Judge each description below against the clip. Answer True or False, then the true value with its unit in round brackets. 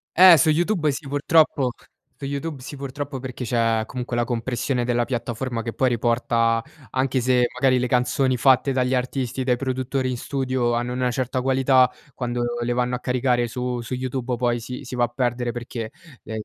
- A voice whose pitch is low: True (125 Hz)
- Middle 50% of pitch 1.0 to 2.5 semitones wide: True (1.6 semitones)